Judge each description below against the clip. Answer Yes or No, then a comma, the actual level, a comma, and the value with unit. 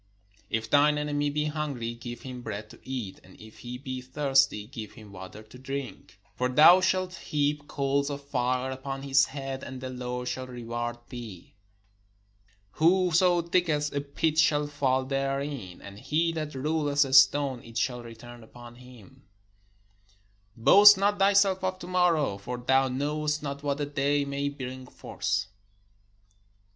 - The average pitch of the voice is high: No, low, 135 Hz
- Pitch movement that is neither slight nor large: Yes, average, 3.2 semitones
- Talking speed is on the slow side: No, average, 155 wpm